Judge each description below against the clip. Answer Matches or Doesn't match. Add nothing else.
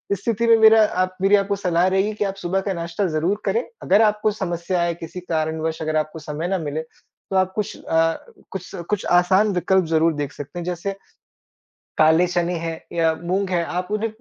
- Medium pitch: Matches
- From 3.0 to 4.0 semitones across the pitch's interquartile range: Matches